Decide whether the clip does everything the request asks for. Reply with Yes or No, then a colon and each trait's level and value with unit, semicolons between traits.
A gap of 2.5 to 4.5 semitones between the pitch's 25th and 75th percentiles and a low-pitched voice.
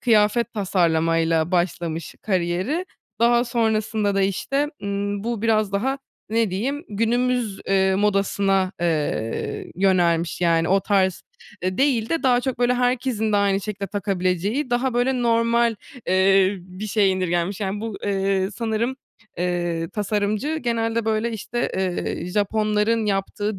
No: average, 3.7 semitones; high, 205 Hz